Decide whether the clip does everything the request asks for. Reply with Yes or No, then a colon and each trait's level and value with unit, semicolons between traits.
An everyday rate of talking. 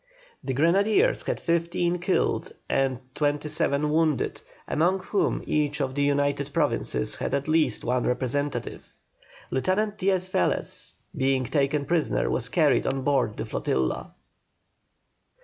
No: slow, 130 wpm